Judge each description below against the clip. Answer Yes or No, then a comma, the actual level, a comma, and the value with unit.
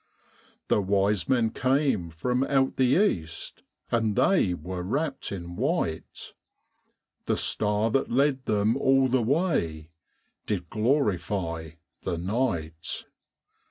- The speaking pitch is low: Yes, low, 110 Hz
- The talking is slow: Yes, slow, 115 wpm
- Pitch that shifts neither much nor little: No, wide, 7.1 semitones